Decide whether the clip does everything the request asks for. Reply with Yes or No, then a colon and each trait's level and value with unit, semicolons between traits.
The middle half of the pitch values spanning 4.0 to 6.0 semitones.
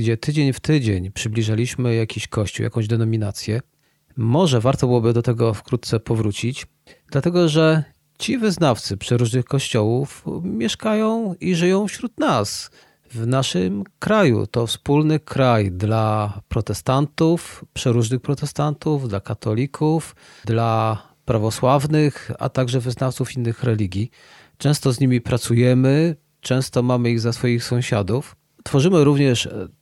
Yes: average, 4.4 semitones